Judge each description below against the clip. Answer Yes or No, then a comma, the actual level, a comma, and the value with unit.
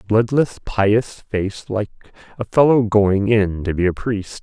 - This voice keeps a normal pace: Yes, average, 165 wpm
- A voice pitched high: No, low, 105 Hz